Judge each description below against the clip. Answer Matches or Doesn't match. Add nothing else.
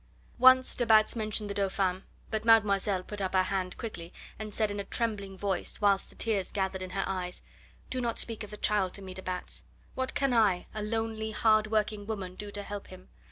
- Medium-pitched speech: Doesn't match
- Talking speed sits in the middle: Doesn't match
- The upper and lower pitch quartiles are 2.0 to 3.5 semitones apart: Matches